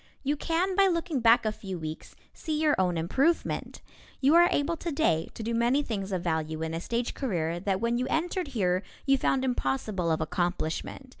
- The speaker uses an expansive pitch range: Yes, wide, 8.9 semitones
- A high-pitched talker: Yes, high, 230 Hz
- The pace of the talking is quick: No, average, 195 wpm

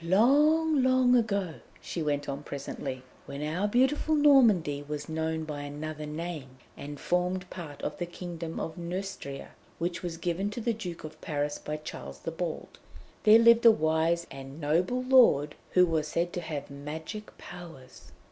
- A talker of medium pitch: Yes, medium, 170 Hz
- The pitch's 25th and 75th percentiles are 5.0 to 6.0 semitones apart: Yes, wide, 5.5 semitones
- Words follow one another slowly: No, average, 165 wpm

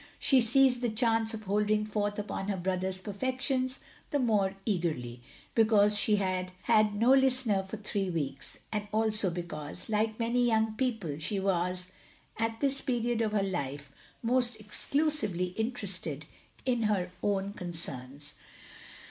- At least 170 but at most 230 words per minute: No, average, 155 wpm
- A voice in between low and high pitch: No, high, 210 Hz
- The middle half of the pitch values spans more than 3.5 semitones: Yes, average, 3.9 semitones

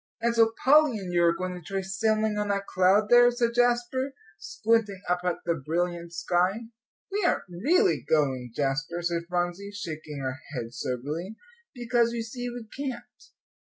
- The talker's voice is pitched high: Yes, high, 195 Hz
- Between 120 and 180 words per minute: Yes, average, 165 wpm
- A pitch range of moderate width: No, wide, 5.7 semitones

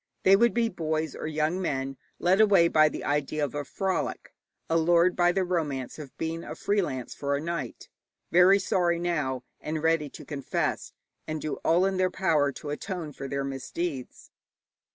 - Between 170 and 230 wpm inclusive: Yes, average, 180 wpm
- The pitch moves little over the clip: No, average, 3.6 semitones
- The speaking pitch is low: No, medium, 160 Hz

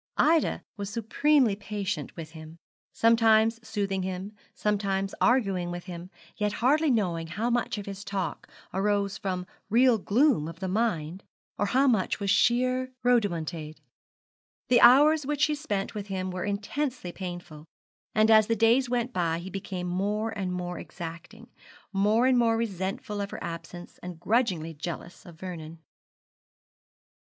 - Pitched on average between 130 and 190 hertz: No, high, 200 Hz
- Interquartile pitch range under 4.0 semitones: No, average, 4.4 semitones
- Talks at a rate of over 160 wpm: No, average, 145 wpm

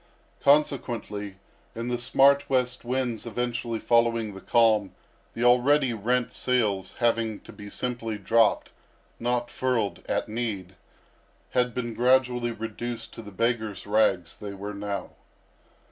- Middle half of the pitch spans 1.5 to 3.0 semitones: Yes, narrow, 2.6 semitones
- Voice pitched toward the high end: No, low, 115 Hz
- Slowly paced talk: Yes, slow, 130 wpm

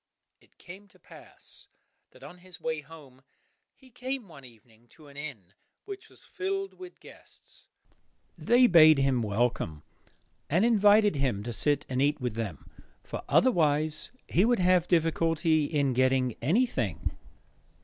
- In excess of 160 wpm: No, average, 145 wpm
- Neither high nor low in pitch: Yes, medium, 155 Hz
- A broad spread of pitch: Yes, wide, 7.4 semitones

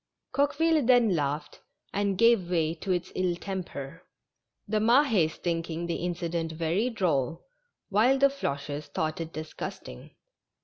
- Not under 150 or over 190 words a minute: No, average, 140 wpm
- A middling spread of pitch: No, wide, 5.7 semitones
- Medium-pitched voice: Yes, medium, 175 Hz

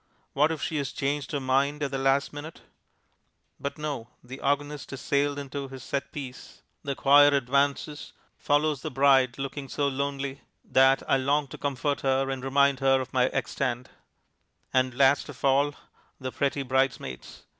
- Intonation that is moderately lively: No, narrow, 1.3 semitones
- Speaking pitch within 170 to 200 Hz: No, medium, 140 Hz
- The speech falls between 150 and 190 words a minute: Yes, average, 170 wpm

